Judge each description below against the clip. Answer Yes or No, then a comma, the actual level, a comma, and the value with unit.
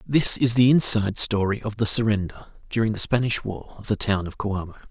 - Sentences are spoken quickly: Yes, fast, 210 wpm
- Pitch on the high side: No, low, 110 Hz